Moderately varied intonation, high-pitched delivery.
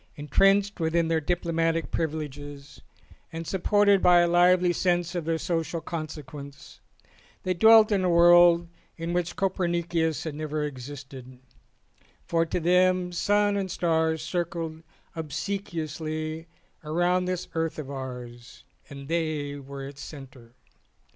No: average, 3.0 semitones; medium, 165 Hz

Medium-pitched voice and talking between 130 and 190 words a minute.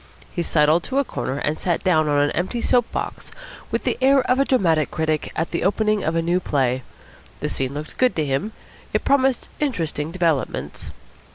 No: medium, 170 Hz; average, 200 wpm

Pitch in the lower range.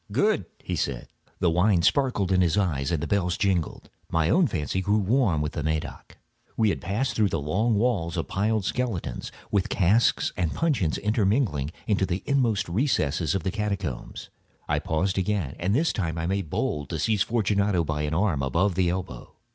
Yes: very low, 95 Hz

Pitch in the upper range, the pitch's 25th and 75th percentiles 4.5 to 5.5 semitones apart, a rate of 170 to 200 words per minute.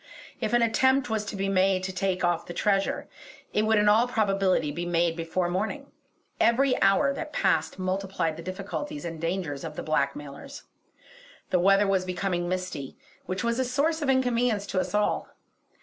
Yes: high, 195 Hz; average, 4.8 semitones; average, 180 wpm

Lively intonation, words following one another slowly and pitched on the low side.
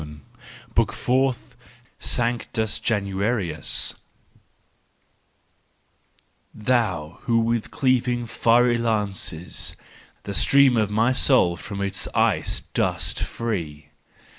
No: average, 3.8 semitones; slow, 90 wpm; low, 110 Hz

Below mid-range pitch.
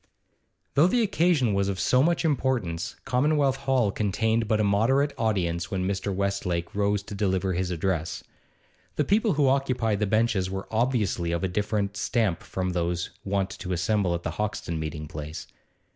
Yes: low, 100 Hz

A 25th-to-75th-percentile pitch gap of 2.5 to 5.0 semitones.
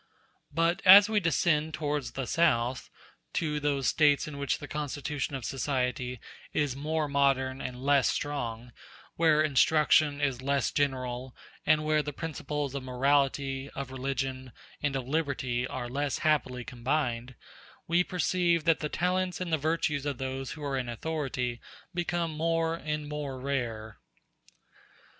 Yes: average, 2.9 semitones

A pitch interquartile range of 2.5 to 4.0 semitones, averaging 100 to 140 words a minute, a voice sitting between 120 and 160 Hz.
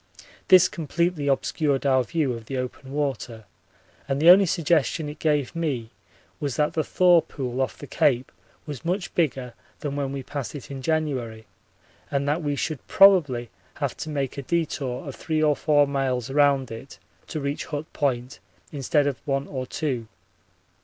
No: average, 3.0 semitones; average, 175 wpm; medium, 140 Hz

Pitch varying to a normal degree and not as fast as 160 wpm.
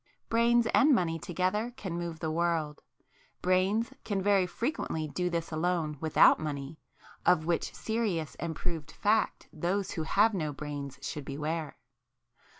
Yes: average, 4.3 semitones; average, 140 wpm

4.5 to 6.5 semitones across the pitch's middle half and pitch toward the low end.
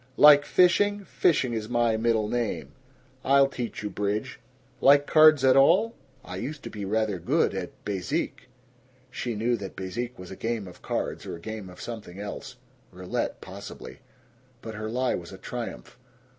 Yes: average, 4.8 semitones; low, 115 Hz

